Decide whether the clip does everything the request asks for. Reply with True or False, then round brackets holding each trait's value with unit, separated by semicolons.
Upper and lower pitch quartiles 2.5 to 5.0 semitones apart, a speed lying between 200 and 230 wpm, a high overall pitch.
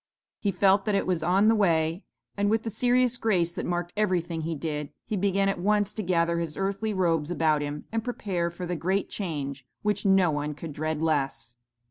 False (4.1 semitones; 205 wpm; 180 Hz)